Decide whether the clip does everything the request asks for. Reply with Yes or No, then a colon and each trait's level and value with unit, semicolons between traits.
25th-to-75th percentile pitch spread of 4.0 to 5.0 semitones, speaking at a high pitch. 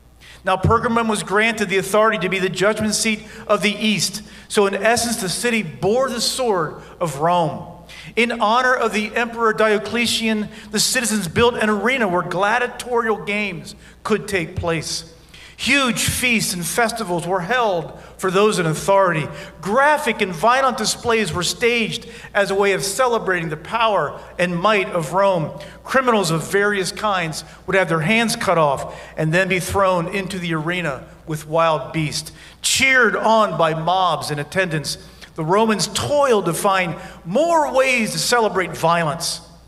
Yes: average, 4.3 semitones; high, 195 Hz